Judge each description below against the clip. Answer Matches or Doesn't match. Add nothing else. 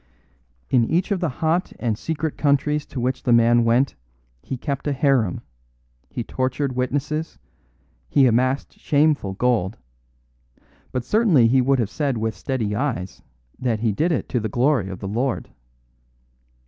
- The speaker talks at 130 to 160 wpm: Matches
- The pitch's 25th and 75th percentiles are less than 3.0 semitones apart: Doesn't match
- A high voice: Doesn't match